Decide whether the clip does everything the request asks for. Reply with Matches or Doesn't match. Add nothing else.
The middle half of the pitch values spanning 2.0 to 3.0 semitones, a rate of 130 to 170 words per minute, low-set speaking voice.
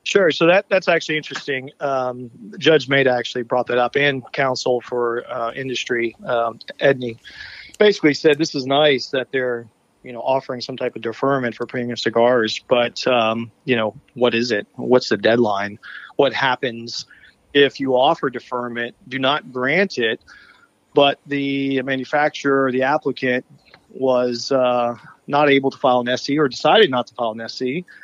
Matches